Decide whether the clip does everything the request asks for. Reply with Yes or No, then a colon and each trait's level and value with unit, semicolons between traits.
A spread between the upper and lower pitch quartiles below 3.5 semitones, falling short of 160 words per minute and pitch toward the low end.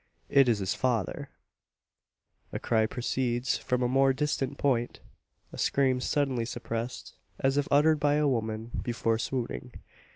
Yes: average, 2.8 semitones; average, 140 wpm; low, 125 Hz